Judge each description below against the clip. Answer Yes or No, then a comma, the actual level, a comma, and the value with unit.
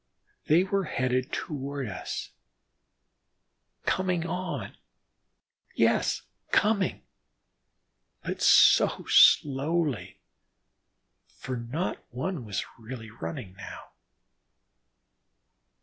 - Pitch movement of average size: No, wide, 6.5 semitones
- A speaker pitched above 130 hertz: Yes, medium, 140 Hz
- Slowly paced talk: Yes, slow, 70 wpm